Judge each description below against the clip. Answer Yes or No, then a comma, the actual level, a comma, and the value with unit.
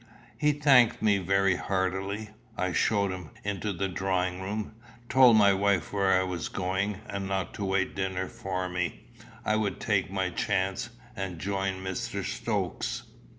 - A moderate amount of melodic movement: No, narrow, 1.5 semitones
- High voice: No, very low, 95 Hz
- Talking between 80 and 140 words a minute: No, average, 155 wpm